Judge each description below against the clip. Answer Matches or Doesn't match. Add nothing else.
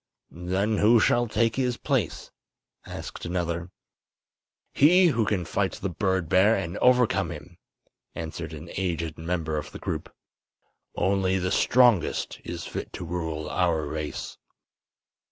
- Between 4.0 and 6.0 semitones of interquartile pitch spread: Matches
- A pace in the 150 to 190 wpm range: Doesn't match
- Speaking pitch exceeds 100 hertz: Doesn't match